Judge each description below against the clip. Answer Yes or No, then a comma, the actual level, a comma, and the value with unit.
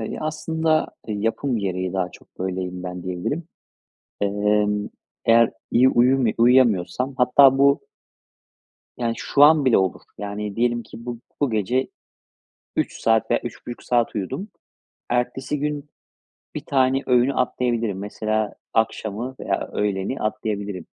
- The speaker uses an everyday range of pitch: Yes, average, 4.2 semitones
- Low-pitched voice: Yes, low, 115 Hz